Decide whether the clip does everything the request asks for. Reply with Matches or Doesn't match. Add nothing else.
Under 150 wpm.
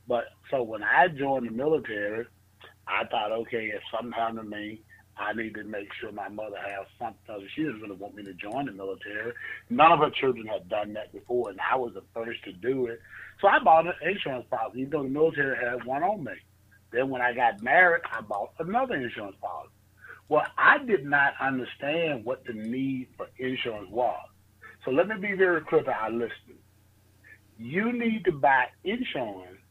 Doesn't match